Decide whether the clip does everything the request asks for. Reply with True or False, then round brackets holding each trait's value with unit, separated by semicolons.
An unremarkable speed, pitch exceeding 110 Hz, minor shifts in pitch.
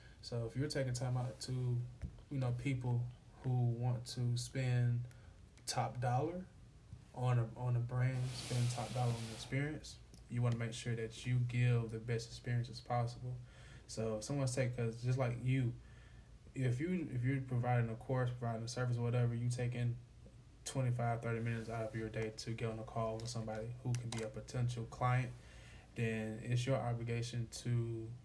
True (180 wpm; 120 Hz; 1.5 semitones)